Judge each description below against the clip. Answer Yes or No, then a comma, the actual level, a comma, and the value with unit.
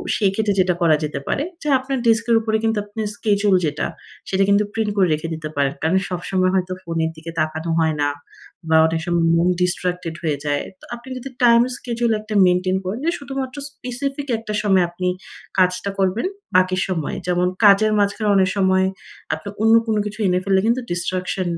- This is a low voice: No, high, 190 Hz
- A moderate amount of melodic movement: Yes, average, 4.0 semitones